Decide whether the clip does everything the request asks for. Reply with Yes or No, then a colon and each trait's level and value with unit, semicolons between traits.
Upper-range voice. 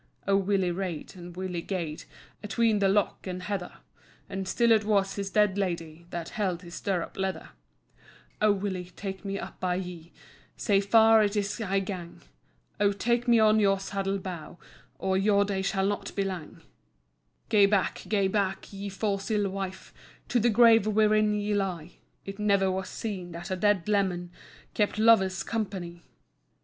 Yes: high, 195 Hz